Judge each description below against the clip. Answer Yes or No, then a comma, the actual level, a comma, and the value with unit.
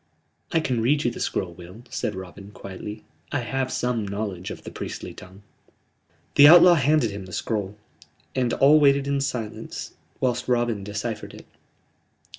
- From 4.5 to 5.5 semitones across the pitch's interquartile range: Yes, average, 5.2 semitones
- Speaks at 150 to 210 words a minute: Yes, average, 160 wpm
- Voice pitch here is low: Yes, low, 120 Hz